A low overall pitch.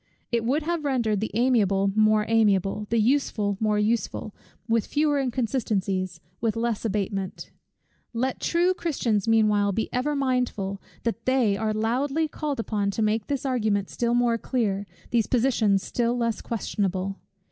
No: high, 225 Hz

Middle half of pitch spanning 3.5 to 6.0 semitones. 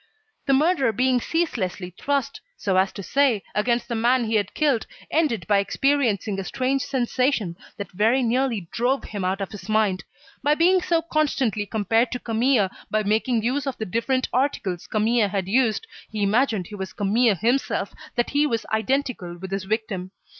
Yes: average, 4.8 semitones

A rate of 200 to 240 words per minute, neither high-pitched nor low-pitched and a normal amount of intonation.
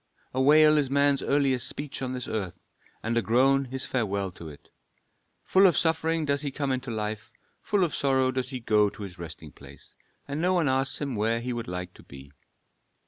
No: fast, 205 wpm; low, 130 Hz; average, 4.5 semitones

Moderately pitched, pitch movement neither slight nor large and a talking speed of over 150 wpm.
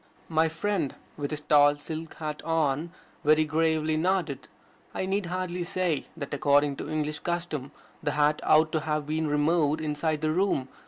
No: medium, 155 Hz; narrow, 1.8 semitones; average, 165 wpm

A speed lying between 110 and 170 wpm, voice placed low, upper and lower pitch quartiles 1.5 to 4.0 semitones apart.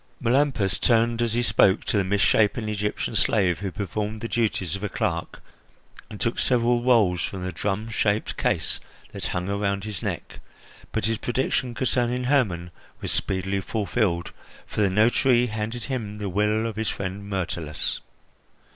Yes: average, 155 wpm; low, 105 Hz; average, 3.3 semitones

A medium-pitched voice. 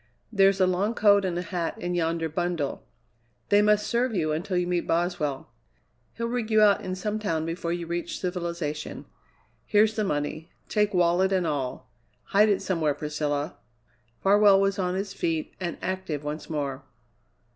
Yes: medium, 180 Hz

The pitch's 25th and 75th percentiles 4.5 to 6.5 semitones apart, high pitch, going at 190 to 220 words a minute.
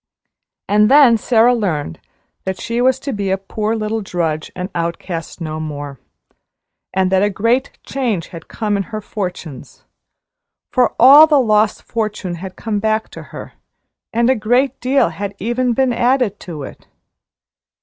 No: average, 4.8 semitones; high, 210 Hz; average, 160 wpm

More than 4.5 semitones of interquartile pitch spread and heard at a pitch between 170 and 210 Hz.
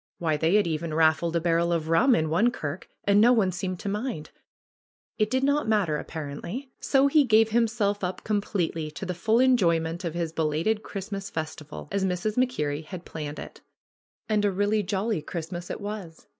Yes: average, 4.9 semitones; medium, 185 Hz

